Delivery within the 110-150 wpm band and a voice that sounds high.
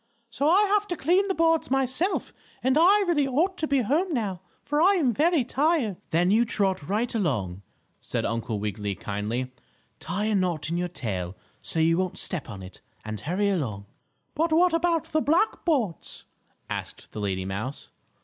No: average, 180 wpm; high, 215 Hz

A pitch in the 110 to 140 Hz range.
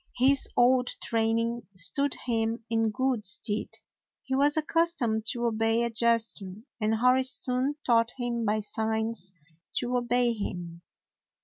No: high, 230 Hz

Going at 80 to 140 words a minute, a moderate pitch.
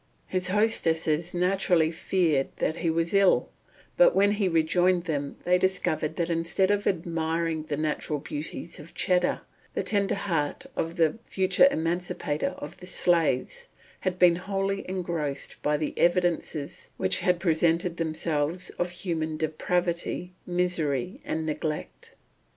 Yes: slow, 135 wpm; medium, 170 Hz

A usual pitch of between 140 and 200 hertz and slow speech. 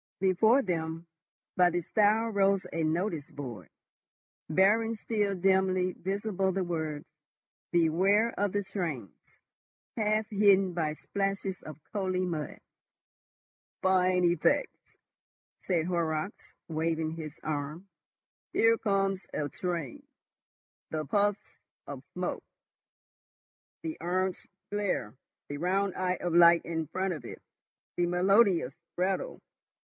Yes: medium, 185 Hz; slow, 110 wpm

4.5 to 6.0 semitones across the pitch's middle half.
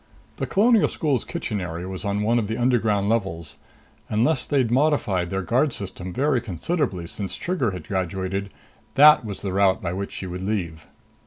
Yes: average, 5.0 semitones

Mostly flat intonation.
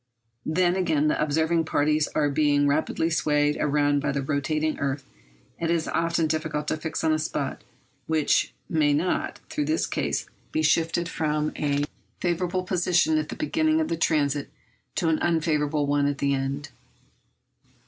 Yes: narrow, 2.2 semitones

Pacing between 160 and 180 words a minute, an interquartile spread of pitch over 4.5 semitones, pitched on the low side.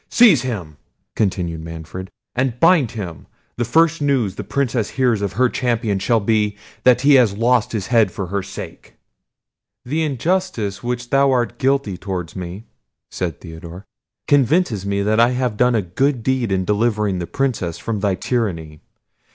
Yes: average, 165 wpm; average, 5.0 semitones; low, 110 Hz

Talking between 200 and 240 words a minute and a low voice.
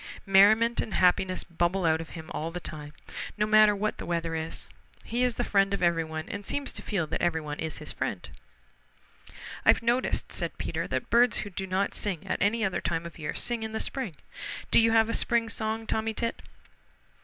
No: fast, 205 wpm; high, 195 Hz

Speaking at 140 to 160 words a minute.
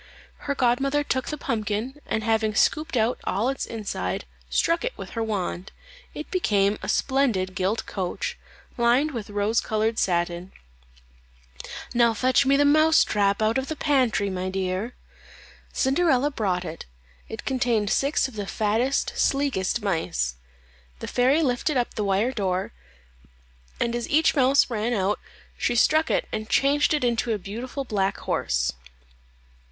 Yes: average, 150 wpm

